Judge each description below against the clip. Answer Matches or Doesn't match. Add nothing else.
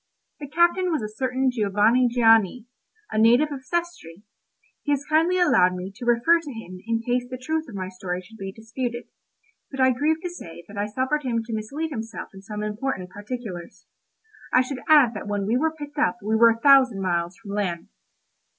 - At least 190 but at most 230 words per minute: Matches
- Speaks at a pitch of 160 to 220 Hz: Doesn't match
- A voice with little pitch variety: Doesn't match